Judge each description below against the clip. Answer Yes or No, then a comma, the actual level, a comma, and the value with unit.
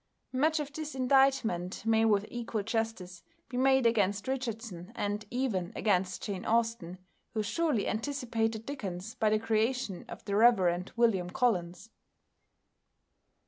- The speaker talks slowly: Yes, slow, 130 wpm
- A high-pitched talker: Yes, high, 225 Hz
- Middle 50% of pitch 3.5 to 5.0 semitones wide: Yes, average, 4.2 semitones